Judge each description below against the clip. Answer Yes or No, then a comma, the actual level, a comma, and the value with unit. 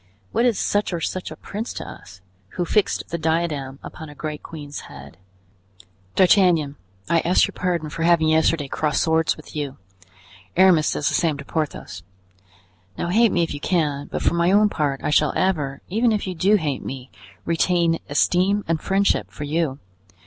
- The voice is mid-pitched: Yes, medium, 165 Hz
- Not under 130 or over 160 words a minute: No, average, 185 wpm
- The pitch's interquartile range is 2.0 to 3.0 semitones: No, average, 3.8 semitones